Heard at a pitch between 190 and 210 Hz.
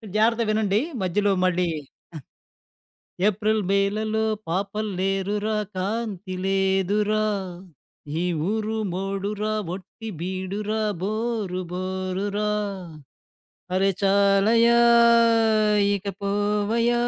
Yes: high, 205 Hz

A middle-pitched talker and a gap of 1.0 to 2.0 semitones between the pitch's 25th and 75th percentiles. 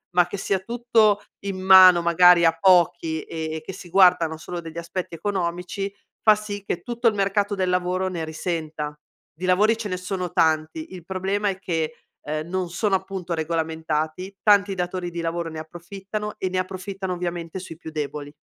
No: medium, 180 Hz; average, 2.8 semitones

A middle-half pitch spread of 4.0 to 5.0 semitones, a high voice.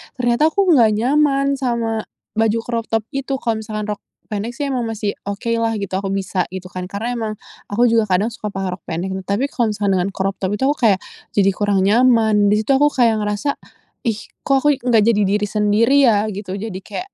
No: average, 3.2 semitones; high, 220 Hz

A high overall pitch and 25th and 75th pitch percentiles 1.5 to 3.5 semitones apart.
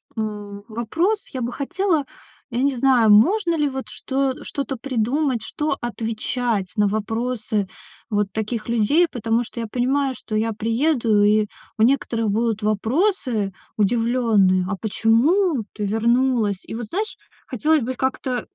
No: high, 235 Hz; average, 3.9 semitones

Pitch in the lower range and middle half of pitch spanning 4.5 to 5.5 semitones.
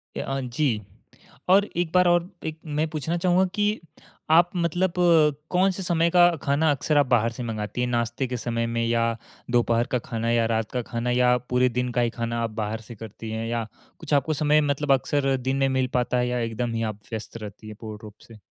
Yes: low, 125 Hz; average, 4.9 semitones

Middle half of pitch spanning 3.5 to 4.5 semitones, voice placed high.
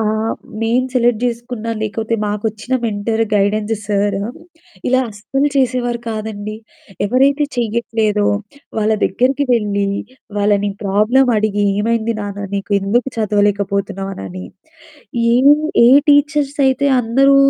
No: average, 3.0 semitones; high, 220 Hz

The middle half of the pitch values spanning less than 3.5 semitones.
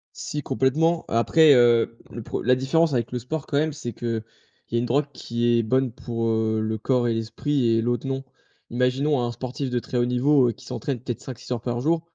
Yes: average, 2.8 semitones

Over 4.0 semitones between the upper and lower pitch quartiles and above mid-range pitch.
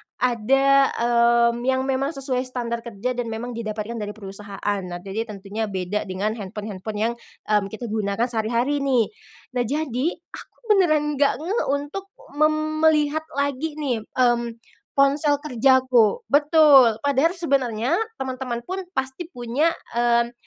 Yes: average, 4.4 semitones; high, 245 Hz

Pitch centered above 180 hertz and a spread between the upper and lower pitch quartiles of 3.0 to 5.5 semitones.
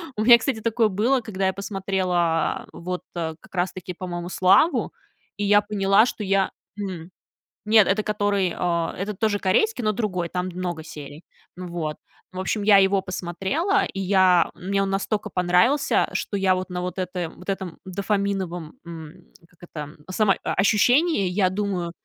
No: high, 190 Hz; narrow, 2.5 semitones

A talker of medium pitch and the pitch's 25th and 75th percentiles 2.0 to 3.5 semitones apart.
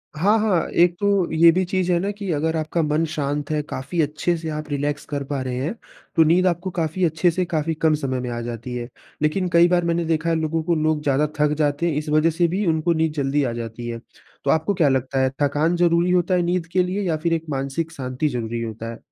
Yes: medium, 160 Hz; average, 3.2 semitones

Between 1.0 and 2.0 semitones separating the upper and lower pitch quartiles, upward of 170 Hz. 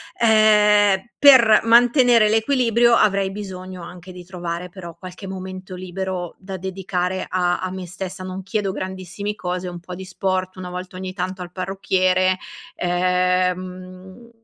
Yes: narrow, 1.6 semitones; medium, 185 Hz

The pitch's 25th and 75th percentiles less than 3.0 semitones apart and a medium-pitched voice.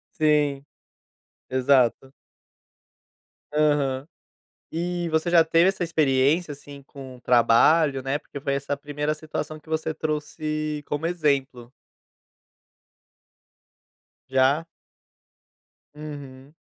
Yes: narrow, 2.6 semitones; medium, 145 Hz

